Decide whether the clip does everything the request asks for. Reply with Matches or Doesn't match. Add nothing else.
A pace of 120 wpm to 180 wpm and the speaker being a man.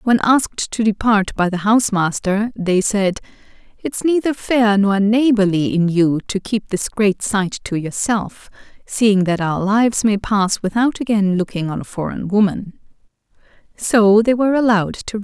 Doesn't match